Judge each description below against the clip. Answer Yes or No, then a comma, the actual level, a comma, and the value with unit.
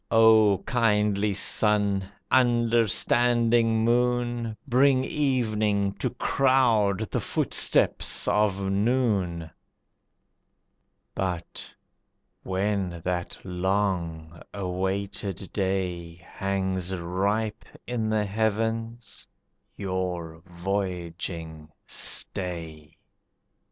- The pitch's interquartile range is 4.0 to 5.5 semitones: No, average, 3.6 semitones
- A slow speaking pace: Yes, slow, 70 wpm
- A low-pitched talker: Yes, low, 100 Hz